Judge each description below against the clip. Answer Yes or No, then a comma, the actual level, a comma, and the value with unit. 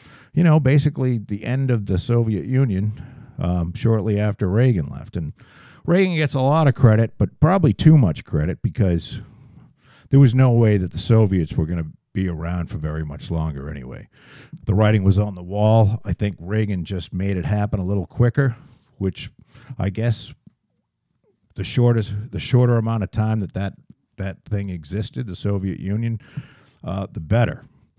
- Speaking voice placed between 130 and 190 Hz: No, low, 110 Hz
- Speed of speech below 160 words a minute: No, average, 175 wpm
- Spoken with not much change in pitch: No, average, 5.1 semitones